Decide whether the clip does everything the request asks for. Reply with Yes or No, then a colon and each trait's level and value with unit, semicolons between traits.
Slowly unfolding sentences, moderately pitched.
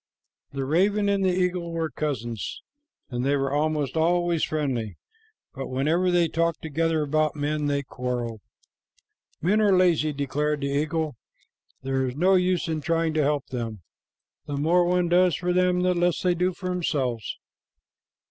No: average, 160 wpm; medium, 155 Hz